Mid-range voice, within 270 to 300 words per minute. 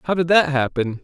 No: medium, 150 Hz; fast, 230 wpm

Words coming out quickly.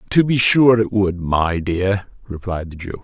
No: average, 195 wpm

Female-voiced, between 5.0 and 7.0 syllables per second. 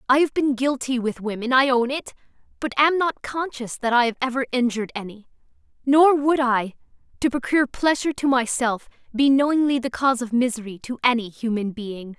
Yes: female; 5.6 syllables/s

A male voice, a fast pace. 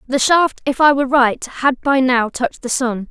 No: female; fast, 230 wpm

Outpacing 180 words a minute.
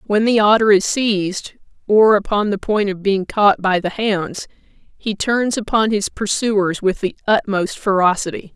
No: average, 170 wpm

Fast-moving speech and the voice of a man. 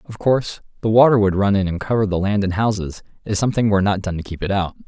Yes: fast, 270 wpm; male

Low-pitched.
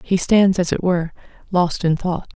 No: medium, 180 Hz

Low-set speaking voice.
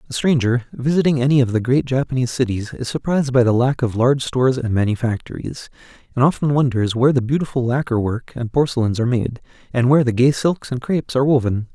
Yes: low, 125 Hz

